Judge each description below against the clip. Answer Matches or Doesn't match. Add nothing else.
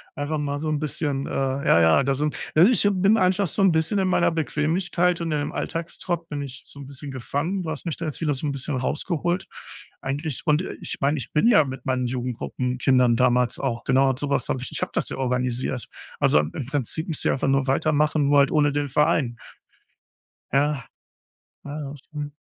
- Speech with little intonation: Doesn't match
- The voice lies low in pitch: Doesn't match